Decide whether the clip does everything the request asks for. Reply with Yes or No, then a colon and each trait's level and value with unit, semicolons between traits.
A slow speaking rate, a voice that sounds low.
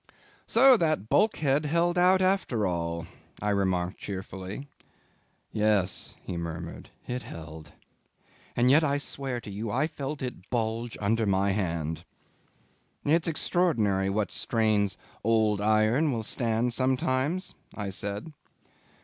Yes: slow, 125 wpm; low, 110 Hz